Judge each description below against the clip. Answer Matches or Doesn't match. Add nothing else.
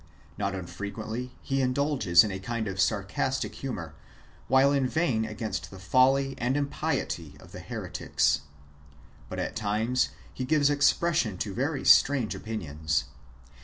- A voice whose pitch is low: Matches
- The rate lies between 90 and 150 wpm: Matches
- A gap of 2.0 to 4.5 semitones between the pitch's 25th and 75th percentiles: Doesn't match